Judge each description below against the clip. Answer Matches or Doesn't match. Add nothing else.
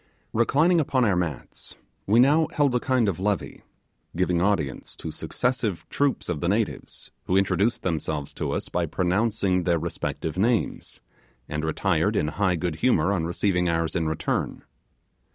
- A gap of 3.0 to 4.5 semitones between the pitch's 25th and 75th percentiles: Doesn't match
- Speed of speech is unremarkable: Matches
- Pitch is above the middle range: Doesn't match